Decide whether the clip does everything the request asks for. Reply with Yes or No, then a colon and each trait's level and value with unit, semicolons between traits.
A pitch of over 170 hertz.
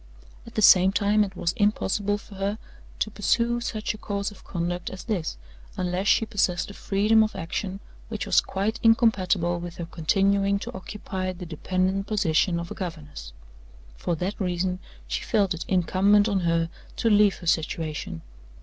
Yes: high, 190 Hz